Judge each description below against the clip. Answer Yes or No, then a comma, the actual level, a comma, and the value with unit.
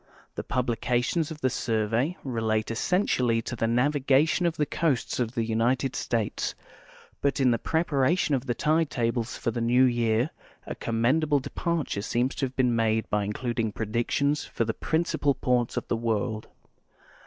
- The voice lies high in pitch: No, low, 125 Hz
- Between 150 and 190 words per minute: Yes, average, 170 wpm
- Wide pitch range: No, average, 3.7 semitones